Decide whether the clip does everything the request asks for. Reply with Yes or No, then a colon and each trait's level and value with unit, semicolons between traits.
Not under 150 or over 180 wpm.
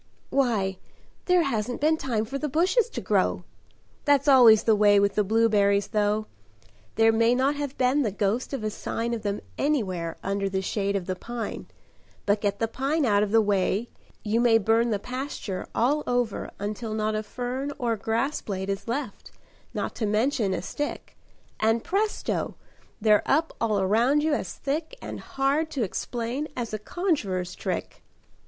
Yes: average, 175 wpm